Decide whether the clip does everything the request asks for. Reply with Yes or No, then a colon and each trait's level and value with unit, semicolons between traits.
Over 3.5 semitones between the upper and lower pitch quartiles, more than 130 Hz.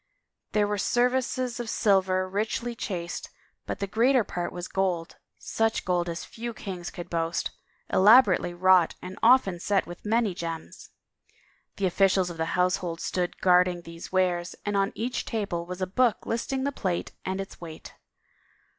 Yes: average, 3.9 semitones; high, 190 Hz